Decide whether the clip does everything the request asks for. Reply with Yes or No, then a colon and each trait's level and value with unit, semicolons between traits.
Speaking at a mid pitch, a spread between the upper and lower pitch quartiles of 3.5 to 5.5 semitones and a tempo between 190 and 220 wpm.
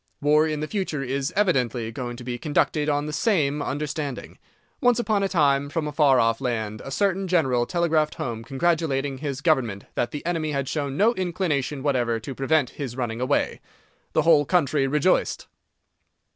No: medium, 145 Hz; average, 3.8 semitones; average, 175 wpm